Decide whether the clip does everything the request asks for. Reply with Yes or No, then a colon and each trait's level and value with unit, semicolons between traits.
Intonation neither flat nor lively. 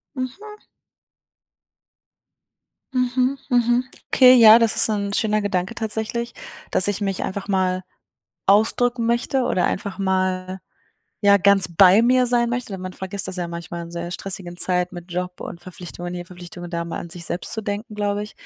Yes: average, 4.3 semitones